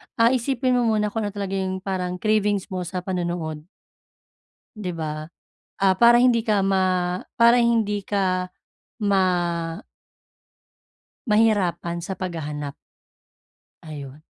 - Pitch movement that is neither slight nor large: Yes, average, 3.3 semitones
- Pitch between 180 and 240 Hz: Yes, high, 190 Hz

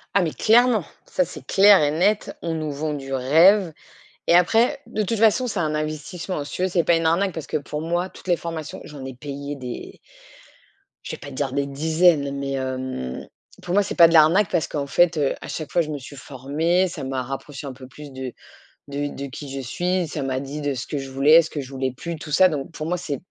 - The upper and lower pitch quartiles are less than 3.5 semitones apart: No, average, 4.1 semitones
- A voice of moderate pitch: Yes, medium, 155 Hz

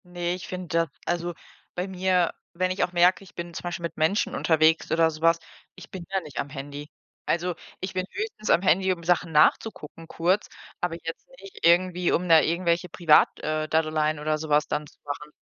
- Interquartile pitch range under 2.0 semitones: No, narrow, 2.4 semitones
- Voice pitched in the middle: Yes, medium, 170 Hz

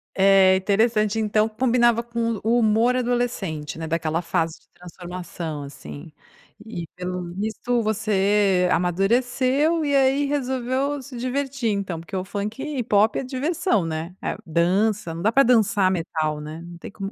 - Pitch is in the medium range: No, high, 210 Hz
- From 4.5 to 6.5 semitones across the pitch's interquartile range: Yes, wide, 5.6 semitones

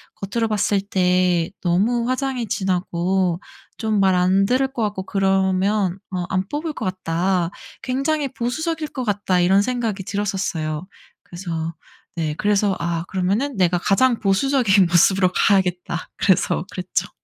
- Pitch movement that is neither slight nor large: Yes, average, 3.7 semitones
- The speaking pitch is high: Yes, high, 195 Hz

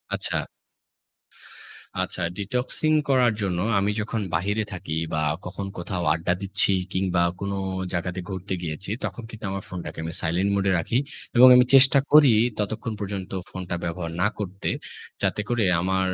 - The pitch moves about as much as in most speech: Yes, average, 3.4 semitones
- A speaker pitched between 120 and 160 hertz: No, very low, 95 Hz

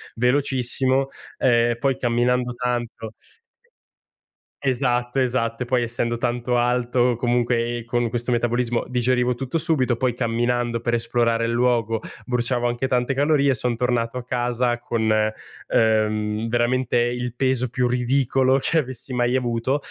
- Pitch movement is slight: Yes, narrow, 1.2 semitones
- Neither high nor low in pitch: No, low, 120 Hz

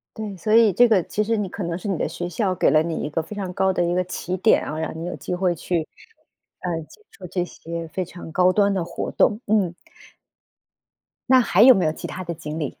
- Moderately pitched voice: Yes, medium, 180 Hz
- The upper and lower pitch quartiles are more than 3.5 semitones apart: No, average, 3.2 semitones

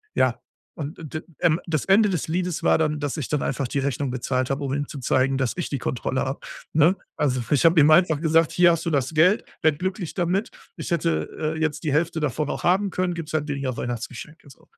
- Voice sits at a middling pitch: Yes, medium, 155 Hz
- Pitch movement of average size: Yes, average, 3.7 semitones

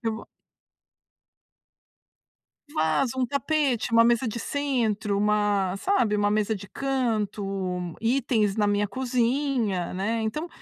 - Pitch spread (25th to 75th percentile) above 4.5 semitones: No, average, 3.9 semitones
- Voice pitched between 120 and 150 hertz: No, high, 225 Hz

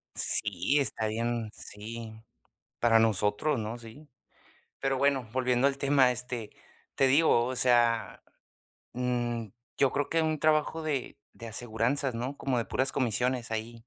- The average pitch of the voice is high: No, low, 120 Hz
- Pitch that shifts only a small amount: No, average, 3.2 semitones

